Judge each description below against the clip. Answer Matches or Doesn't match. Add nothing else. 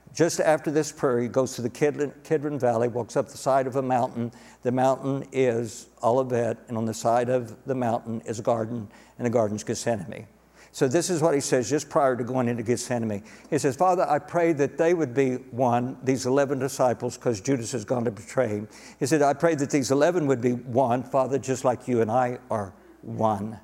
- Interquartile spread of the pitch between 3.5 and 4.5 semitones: Doesn't match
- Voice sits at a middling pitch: Doesn't match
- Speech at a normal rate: Doesn't match